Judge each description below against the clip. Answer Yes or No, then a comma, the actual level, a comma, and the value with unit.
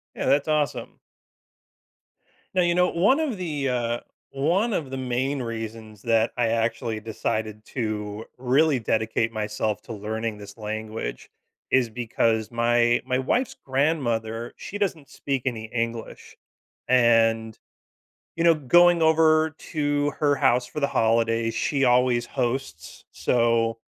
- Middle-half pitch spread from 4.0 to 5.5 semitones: Yes, average, 4.3 semitones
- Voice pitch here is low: Yes, low, 120 Hz